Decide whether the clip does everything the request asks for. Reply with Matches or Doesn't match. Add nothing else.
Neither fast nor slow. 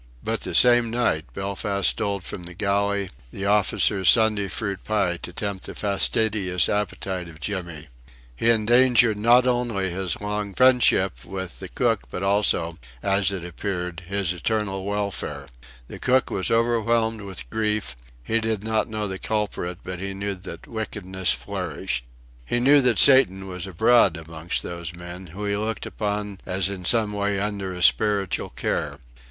Matches